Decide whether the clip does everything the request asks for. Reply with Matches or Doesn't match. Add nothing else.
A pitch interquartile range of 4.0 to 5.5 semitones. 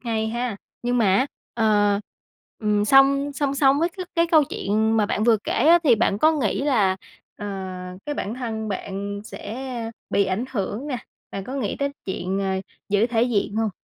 Matches